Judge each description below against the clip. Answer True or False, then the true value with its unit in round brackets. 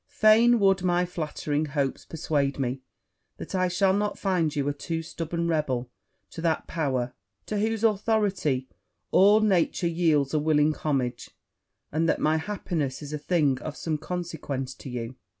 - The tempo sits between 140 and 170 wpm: True (160 wpm)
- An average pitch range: True (4.4 semitones)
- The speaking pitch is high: False (160 Hz)